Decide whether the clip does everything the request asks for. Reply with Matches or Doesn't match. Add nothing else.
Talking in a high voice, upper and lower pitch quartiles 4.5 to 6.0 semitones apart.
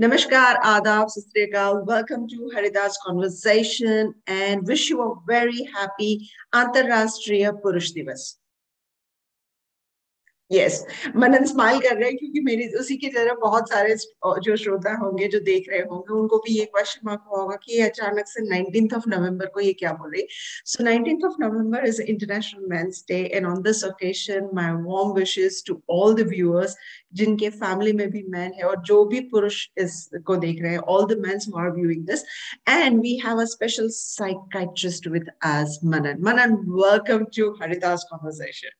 Doesn't match